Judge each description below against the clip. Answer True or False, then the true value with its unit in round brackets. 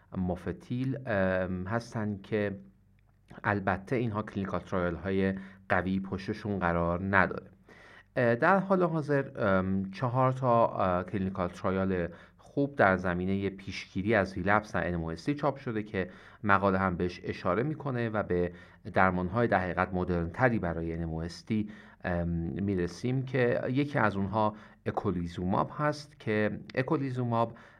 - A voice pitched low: True (100 Hz)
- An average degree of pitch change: True (4.2 semitones)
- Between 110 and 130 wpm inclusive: True (115 wpm)